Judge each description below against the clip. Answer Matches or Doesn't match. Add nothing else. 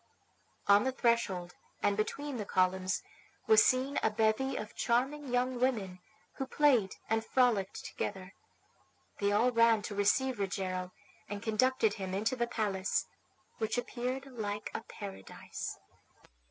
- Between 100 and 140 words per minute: Matches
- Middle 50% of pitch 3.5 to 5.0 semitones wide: Matches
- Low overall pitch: Doesn't match